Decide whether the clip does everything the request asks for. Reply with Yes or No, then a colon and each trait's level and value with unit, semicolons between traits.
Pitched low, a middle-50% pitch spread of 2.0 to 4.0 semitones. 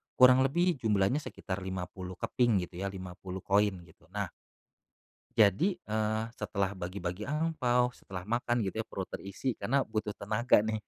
No: low, 100 Hz; average, 4.5 semitones